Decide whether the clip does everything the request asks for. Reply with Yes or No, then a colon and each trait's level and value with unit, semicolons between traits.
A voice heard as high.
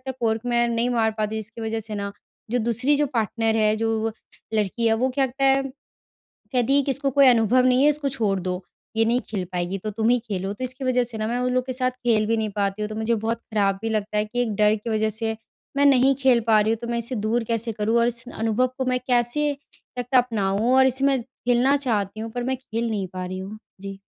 Yes: high, 230 Hz